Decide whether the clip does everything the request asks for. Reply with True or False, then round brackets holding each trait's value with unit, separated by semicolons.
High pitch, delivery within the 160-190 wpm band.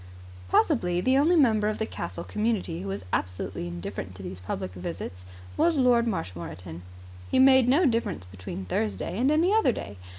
False (180 Hz; 170 wpm)